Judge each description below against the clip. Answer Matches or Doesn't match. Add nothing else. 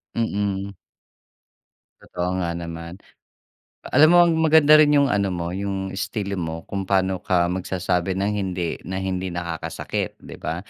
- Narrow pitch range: Matches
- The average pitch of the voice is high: Doesn't match